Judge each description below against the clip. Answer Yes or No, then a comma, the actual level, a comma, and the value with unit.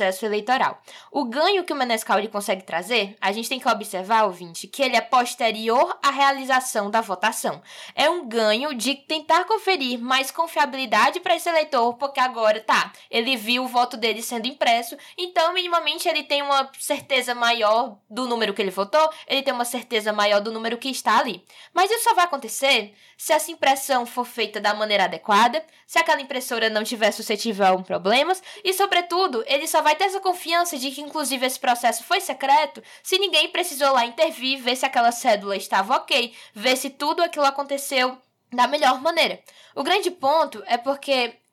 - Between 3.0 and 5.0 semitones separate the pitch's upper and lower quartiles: No, wide, 5.4 semitones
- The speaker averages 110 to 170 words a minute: No, fast, 185 wpm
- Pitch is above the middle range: Yes, very high, 260 Hz